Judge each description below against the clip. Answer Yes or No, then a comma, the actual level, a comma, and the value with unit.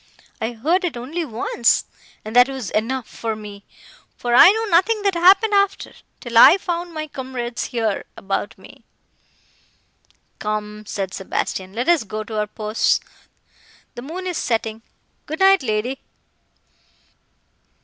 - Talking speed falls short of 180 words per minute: Yes, average, 140 wpm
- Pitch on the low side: No, high, 245 Hz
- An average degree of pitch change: No, wide, 8.1 semitones